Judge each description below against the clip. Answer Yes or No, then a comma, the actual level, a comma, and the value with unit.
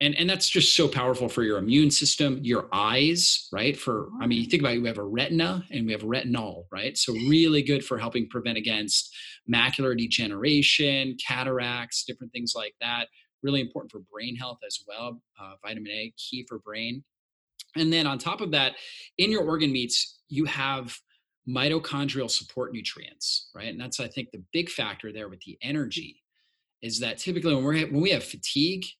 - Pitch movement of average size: Yes, average, 4.3 semitones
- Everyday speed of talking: Yes, average, 190 wpm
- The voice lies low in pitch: Yes, low, 130 Hz